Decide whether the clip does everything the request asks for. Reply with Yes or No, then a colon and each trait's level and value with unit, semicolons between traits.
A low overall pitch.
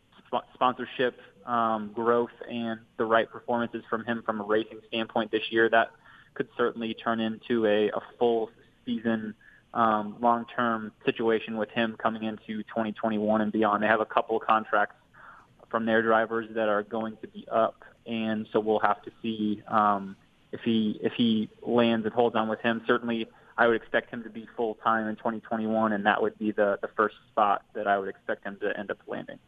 Yes: low, 115 Hz